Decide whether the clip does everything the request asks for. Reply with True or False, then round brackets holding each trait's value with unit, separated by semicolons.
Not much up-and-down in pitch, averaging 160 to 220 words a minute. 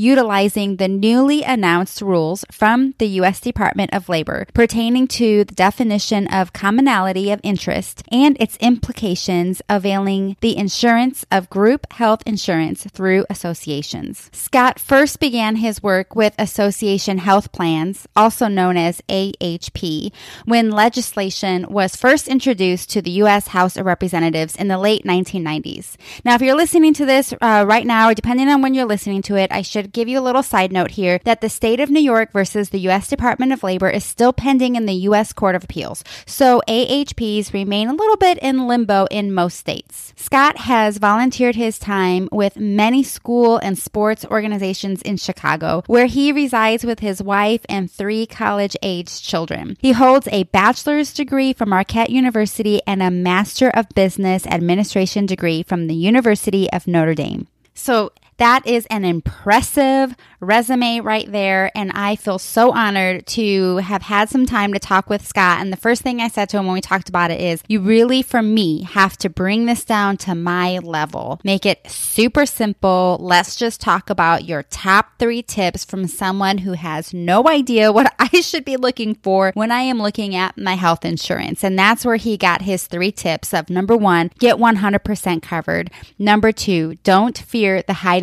False (3.8 semitones; 180 wpm)